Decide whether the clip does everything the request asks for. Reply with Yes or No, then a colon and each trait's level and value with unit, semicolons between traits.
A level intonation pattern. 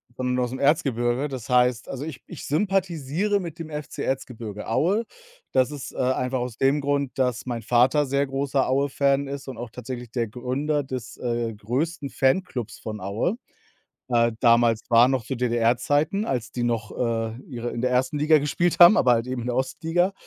No: average, 3.2 semitones